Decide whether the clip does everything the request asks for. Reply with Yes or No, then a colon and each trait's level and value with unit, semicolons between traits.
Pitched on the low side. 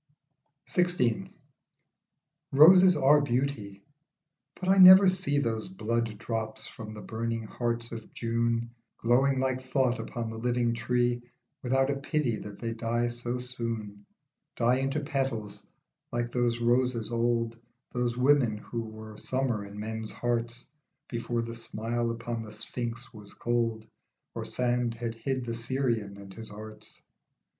Yes: low, 120 Hz